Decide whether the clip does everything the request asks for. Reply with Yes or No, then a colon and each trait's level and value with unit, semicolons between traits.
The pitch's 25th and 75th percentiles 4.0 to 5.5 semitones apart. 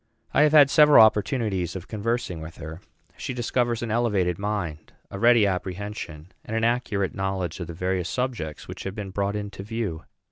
Yes: average, 4.4 semitones